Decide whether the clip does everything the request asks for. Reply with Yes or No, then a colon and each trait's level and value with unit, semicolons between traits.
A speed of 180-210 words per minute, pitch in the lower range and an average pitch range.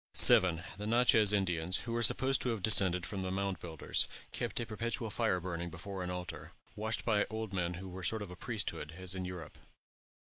Yes: fast, 205 wpm; very low, 95 Hz; average, 3.5 semitones